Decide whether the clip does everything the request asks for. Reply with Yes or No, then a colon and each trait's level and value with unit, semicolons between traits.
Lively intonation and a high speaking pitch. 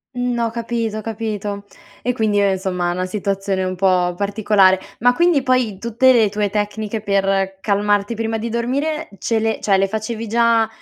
No: average, 2.9 semitones; high, 215 Hz